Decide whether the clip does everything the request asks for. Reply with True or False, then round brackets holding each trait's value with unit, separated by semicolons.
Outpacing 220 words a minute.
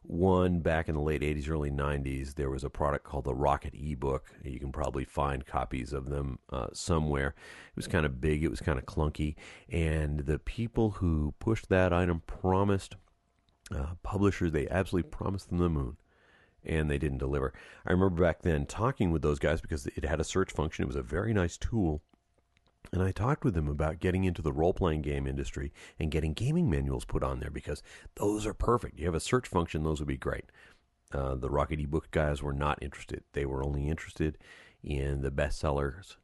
False (205 wpm)